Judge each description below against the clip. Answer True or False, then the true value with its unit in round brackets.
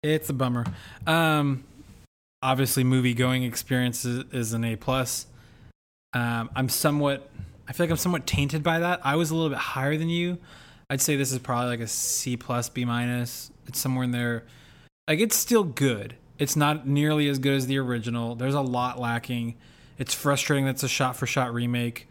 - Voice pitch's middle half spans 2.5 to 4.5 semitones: True (2.8 semitones)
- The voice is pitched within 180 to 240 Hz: False (130 Hz)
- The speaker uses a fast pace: False (190 wpm)